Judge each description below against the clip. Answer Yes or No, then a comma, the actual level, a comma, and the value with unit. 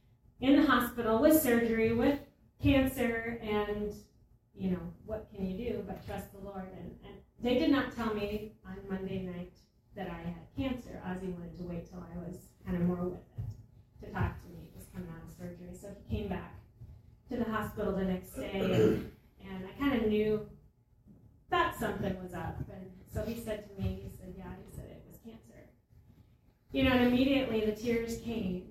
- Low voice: No, high, 195 Hz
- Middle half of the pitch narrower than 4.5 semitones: No, average, 5.1 semitones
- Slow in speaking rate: No, average, 200 wpm